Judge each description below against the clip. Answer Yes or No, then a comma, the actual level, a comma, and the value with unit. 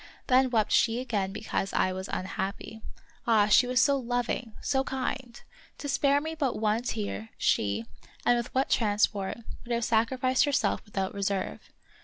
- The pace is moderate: Yes, average, 160 wpm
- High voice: Yes, high, 230 Hz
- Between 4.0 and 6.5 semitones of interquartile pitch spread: Yes, average, 4.4 semitones